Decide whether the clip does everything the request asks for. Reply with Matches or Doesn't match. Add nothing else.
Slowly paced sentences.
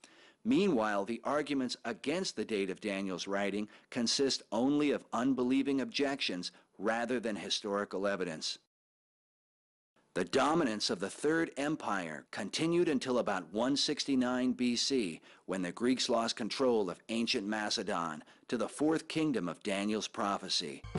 Matches